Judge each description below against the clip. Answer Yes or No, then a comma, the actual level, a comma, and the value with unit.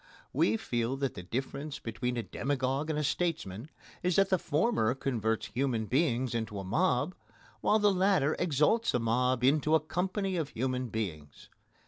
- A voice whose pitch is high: No, low, 135 Hz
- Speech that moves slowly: No, average, 165 wpm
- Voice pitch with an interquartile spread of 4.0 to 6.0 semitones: Yes, wide, 5.6 semitones